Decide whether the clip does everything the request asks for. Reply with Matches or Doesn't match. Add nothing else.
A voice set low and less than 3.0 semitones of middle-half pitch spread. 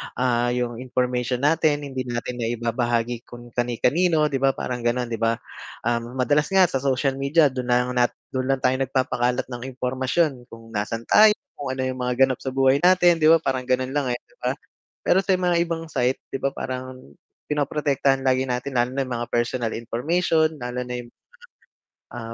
Matches